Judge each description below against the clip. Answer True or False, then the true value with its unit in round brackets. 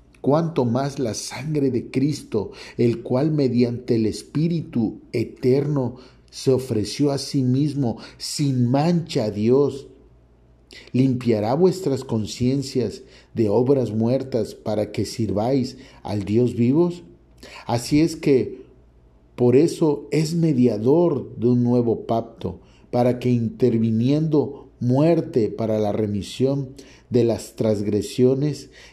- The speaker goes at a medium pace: False (110 wpm)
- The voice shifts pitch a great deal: False (3.7 semitones)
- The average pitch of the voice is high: False (125 Hz)